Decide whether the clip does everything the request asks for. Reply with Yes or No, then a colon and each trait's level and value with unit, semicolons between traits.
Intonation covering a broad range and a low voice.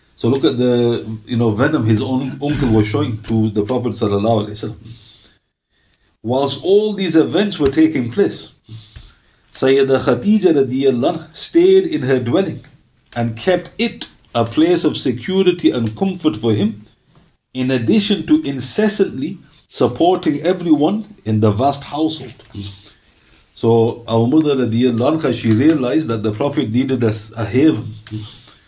Yes: wide, 5.8 semitones; low, 125 Hz